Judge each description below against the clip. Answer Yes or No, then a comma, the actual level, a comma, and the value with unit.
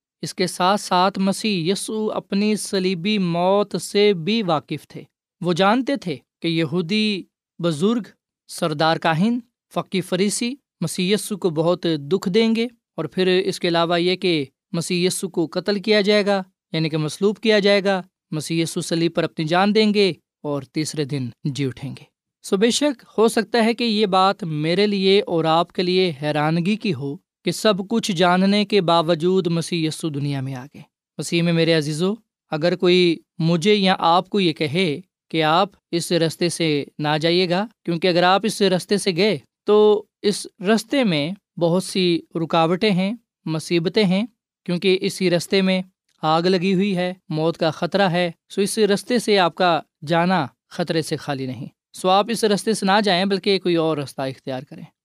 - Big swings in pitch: No, average, 3.5 semitones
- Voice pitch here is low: No, medium, 185 Hz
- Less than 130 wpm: No, average, 180 wpm